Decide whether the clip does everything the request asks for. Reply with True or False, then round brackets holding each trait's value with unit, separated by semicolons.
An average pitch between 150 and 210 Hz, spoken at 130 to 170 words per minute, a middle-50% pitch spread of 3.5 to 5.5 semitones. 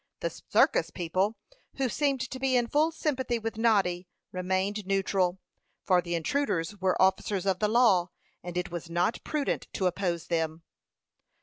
True (190 Hz; 160 wpm; 4.8 semitones)